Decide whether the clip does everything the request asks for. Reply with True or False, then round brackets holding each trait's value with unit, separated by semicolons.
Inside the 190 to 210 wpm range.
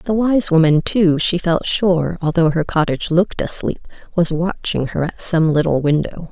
False (180 wpm)